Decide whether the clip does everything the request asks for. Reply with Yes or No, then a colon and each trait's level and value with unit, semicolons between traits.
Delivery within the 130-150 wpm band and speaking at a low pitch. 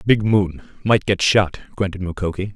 Yes: average, 140 wpm; very low, 95 Hz